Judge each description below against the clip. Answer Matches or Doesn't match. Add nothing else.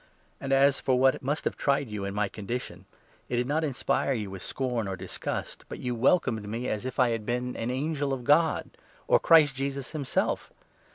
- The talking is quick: Matches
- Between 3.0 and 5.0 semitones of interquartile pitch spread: Matches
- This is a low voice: Matches